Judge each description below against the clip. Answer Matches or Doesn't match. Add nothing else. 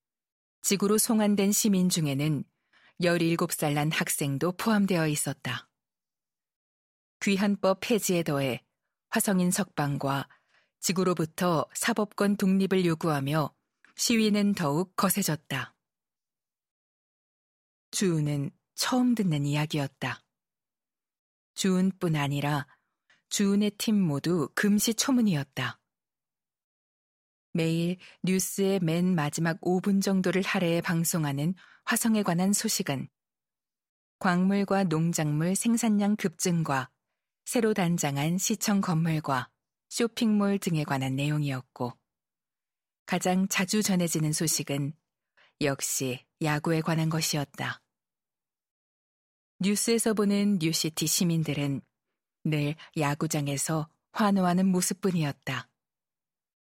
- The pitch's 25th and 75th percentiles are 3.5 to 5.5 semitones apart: Matches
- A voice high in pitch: Doesn't match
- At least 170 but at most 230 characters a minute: Matches